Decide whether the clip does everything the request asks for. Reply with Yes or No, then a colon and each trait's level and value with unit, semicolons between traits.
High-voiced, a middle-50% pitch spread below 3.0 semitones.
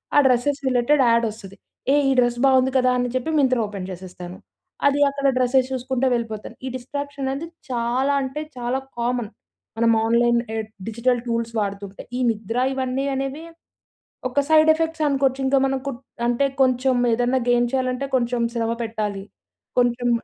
Yes: very high, 250 Hz; narrow, 2.4 semitones